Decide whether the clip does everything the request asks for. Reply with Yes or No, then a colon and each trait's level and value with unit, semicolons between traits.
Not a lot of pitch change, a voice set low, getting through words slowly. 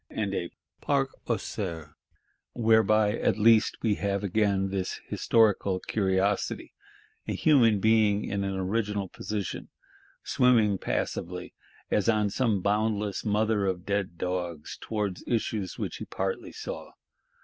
Yes: narrow, 2.3 semitones; low, 105 Hz; slow, 125 wpm